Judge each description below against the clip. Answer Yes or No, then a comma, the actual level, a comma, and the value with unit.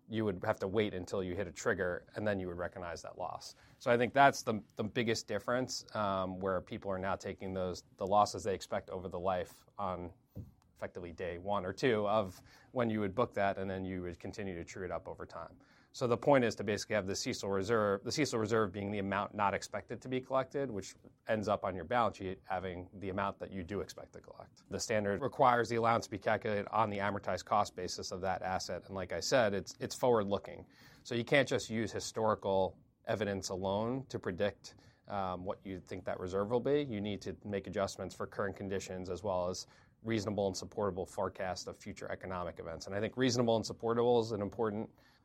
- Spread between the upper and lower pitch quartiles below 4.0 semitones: Yes, average, 3.5 semitones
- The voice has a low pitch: Yes, low, 105 Hz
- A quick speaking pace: Yes, fast, 225 wpm